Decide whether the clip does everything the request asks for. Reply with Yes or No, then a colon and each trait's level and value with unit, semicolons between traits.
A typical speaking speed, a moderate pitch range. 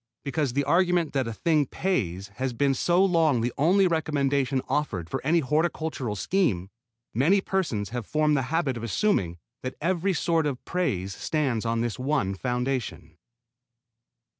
No: average, 155 wpm; wide, 5.9 semitones